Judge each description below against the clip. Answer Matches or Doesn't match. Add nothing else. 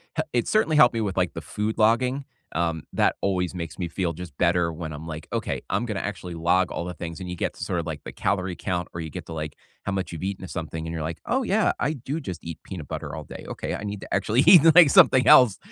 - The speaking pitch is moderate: Doesn't match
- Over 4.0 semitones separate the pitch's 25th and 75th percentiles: Matches